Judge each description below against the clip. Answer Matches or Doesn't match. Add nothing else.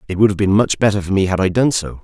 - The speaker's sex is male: Matches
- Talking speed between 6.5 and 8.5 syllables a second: Matches